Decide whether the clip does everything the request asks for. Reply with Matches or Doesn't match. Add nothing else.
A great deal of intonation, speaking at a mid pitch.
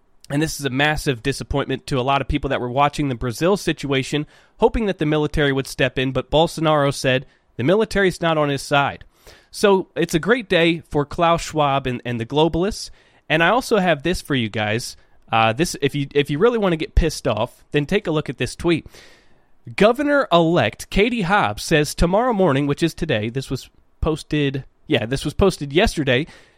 Doesn't match